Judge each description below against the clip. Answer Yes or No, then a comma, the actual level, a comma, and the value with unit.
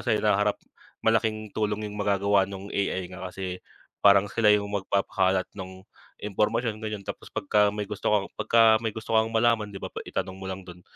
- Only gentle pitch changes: Yes, narrow, 2.0 semitones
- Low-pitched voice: Yes, low, 105 Hz